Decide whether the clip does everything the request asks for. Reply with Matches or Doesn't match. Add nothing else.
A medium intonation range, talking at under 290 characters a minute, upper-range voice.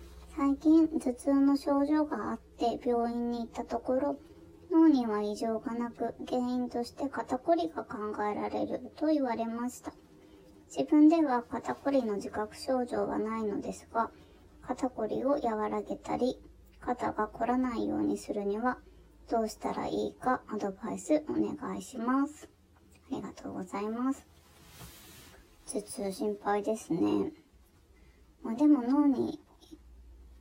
Matches